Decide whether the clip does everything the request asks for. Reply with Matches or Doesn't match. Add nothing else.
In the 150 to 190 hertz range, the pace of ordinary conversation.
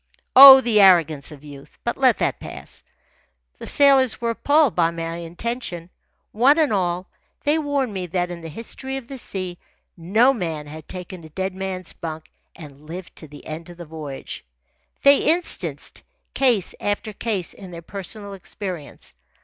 Matches